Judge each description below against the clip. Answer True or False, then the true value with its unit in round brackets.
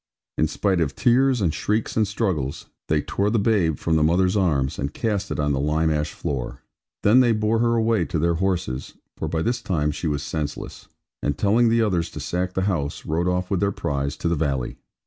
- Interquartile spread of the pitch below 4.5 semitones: False (5.6 semitones)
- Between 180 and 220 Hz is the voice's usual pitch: False (90 Hz)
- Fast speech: True (220 wpm)